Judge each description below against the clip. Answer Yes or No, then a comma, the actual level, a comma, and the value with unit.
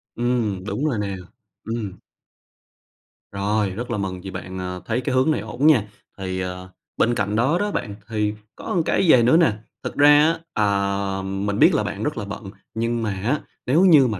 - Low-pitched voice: Yes, low, 105 Hz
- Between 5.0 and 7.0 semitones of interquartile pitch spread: No, average, 4.1 semitones